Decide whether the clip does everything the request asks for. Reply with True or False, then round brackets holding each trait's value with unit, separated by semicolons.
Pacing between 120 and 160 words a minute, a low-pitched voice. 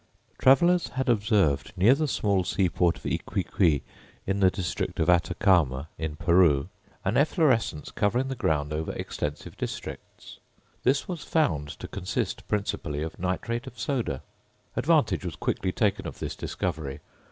True (140 wpm; 95 Hz)